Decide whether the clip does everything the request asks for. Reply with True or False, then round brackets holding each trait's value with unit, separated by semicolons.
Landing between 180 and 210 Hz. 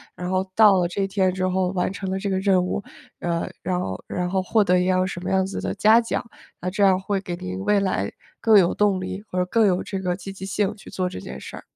True (190 Hz)